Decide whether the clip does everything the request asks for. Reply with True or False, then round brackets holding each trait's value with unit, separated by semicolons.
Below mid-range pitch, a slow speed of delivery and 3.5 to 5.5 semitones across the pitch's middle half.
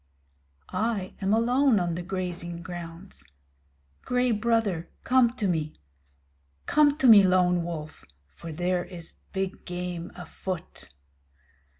False (185 Hz; 115 wpm; 4.5 semitones)